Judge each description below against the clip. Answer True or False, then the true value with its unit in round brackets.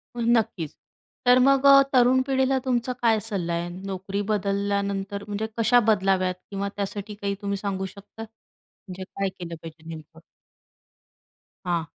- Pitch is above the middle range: True (200 Hz)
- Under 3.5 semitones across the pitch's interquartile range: True (3.1 semitones)